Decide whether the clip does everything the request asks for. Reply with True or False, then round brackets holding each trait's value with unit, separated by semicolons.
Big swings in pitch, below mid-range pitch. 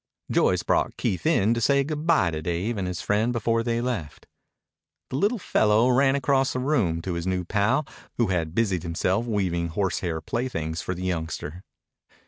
True (6.4 semitones; 105 Hz)